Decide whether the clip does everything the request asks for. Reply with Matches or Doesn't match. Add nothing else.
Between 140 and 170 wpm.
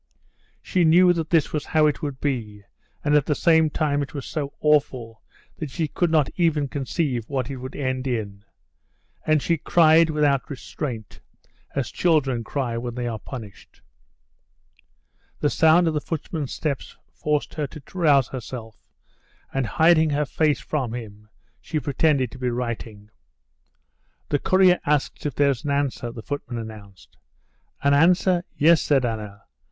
Matches